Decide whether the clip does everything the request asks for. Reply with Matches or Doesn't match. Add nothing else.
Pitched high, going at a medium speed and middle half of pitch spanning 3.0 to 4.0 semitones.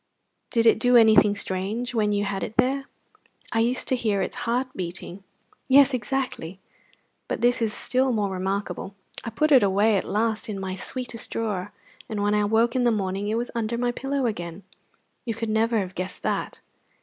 Matches